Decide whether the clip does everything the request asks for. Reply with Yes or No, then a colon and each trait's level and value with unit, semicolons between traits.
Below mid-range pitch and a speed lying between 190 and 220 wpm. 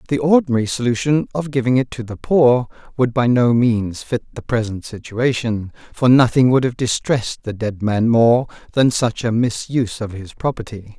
No: low, 120 Hz; average, 180 wpm